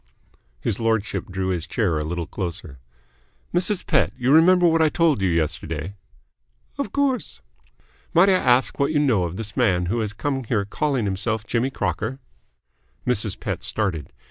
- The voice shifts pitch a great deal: Yes, wide, 7.4 semitones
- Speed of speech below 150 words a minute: No, average, 165 wpm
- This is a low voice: Yes, low, 110 Hz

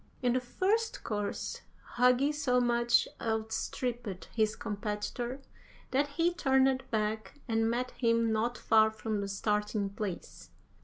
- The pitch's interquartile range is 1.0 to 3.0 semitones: Yes, average, 2.7 semitones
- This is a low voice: No, high, 230 Hz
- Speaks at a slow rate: Yes, slow, 125 wpm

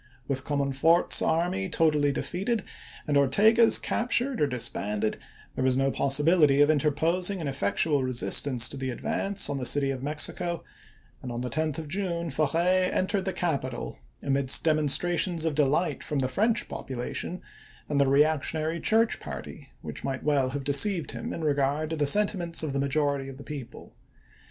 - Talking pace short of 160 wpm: No, average, 175 wpm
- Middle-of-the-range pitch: Yes, medium, 150 Hz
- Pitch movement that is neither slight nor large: Yes, average, 4.0 semitones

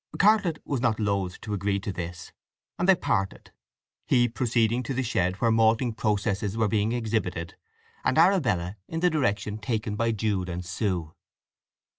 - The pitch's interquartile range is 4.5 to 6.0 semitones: No, average, 3.7 semitones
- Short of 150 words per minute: No, average, 155 wpm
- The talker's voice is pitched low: Yes, low, 110 Hz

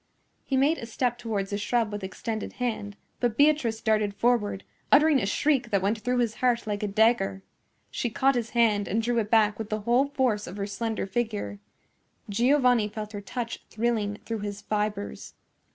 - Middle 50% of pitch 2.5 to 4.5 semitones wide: Yes, average, 2.8 semitones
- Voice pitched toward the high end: Yes, high, 220 Hz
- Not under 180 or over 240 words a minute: Yes, average, 185 wpm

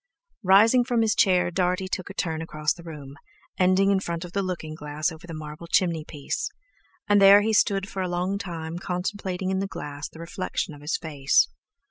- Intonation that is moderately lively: Yes, average, 3.4 semitones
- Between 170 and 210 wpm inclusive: Yes, average, 200 wpm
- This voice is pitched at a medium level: Yes, medium, 180 Hz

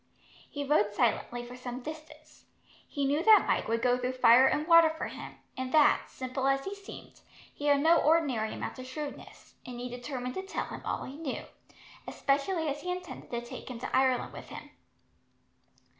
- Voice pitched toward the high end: Yes, very high, 270 Hz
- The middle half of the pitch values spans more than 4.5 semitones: No, average, 3.8 semitones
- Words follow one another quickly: No, average, 190 wpm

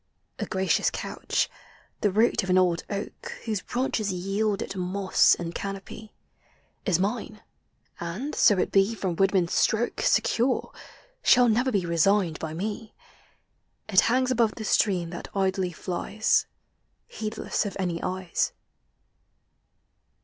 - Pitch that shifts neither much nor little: Yes, average, 3.1 semitones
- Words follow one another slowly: Yes, slow, 130 wpm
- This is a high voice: Yes, high, 195 Hz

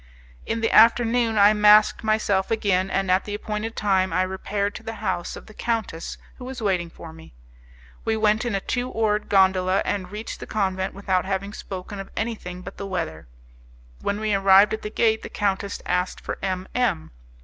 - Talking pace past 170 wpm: Yes, average, 195 wpm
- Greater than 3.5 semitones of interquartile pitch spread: No, narrow, 2.5 semitones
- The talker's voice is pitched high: Yes, high, 200 Hz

